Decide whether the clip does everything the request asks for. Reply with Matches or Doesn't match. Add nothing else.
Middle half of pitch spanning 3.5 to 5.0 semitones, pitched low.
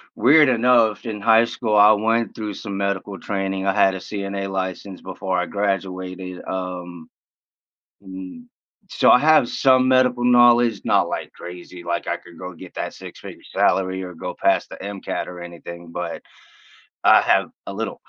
Matches